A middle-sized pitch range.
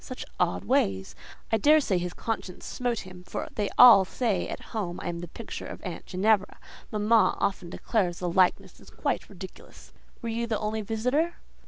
Yes: average, 4.2 semitones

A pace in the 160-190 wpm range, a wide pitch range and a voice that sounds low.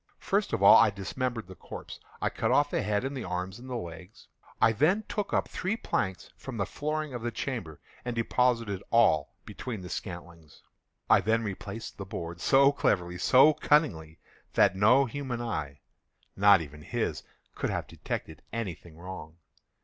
Yes: average, 170 wpm; wide, 6.2 semitones; low, 110 Hz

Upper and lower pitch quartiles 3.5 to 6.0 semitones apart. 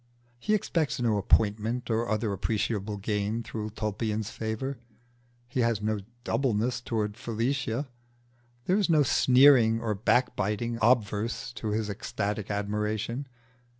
No: narrow, 2.5 semitones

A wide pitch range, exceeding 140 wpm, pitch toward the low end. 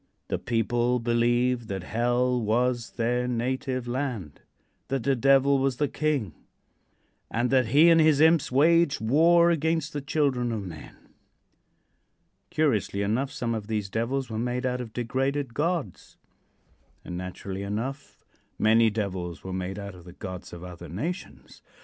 No: average, 4.3 semitones; average, 150 wpm; low, 120 Hz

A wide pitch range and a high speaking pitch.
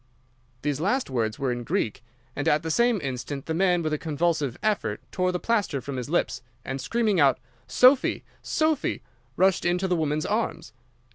No: wide, 6.0 semitones; medium, 160 Hz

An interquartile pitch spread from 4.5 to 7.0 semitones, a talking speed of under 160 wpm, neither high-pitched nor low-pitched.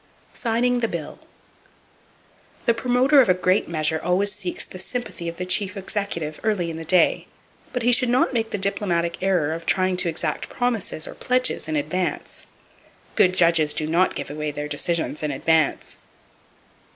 No: average, 5.2 semitones; average, 170 wpm; medium, 180 Hz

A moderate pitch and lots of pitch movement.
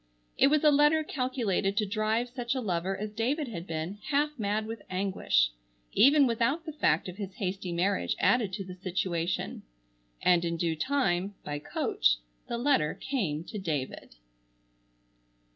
No: high, 200 Hz; wide, 6.2 semitones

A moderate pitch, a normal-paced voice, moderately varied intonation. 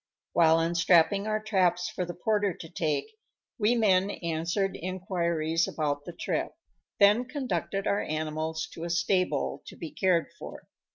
Yes: medium, 175 Hz; average, 150 wpm; average, 3.5 semitones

